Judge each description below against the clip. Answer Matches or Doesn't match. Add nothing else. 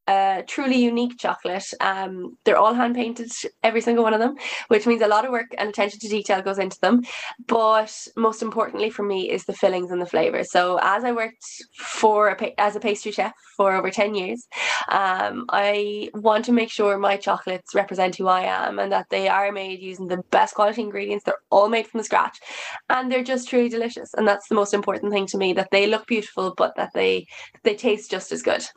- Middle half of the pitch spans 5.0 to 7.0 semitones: Doesn't match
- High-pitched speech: Matches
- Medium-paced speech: Doesn't match